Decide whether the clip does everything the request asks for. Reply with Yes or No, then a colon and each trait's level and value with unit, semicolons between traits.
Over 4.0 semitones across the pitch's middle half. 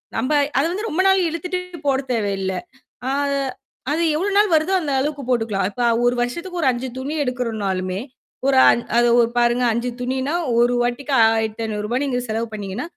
Yes: average, 4.8 semitones